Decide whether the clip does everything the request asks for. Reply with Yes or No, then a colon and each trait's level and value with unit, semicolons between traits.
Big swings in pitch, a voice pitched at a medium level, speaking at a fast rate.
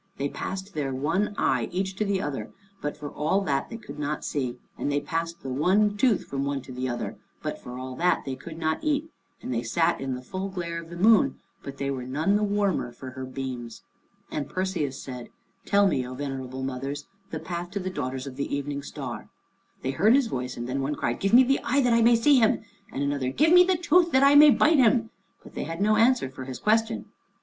Yes: wide, 7.7 semitones; medium, 155 Hz; fast, 235 wpm